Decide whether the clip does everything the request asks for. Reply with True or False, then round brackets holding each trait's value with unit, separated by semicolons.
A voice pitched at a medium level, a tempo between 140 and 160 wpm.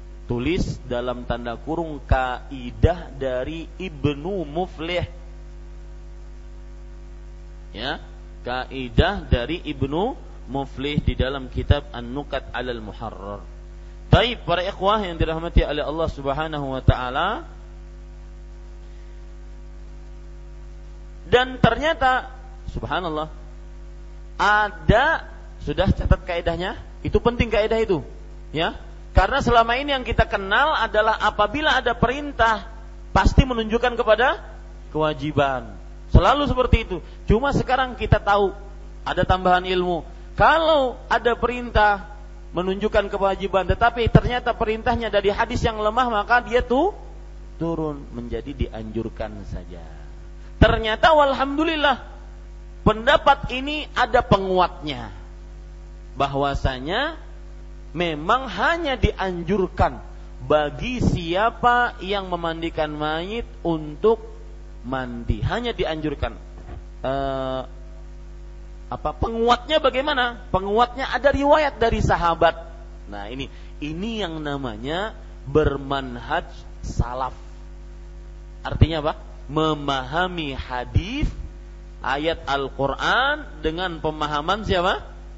False (160 Hz; 90 wpm)